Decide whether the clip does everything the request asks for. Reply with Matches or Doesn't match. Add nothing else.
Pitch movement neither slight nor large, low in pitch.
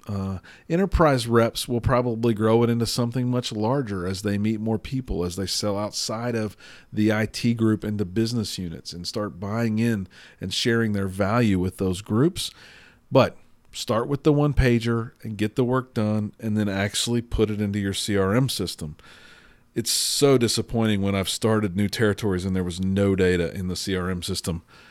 Matches